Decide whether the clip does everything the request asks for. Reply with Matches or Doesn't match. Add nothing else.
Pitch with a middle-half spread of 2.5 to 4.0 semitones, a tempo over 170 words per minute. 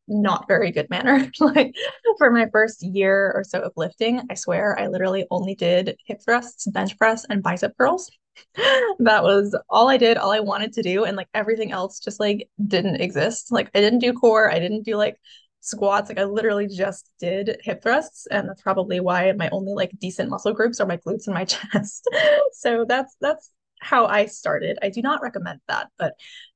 Matches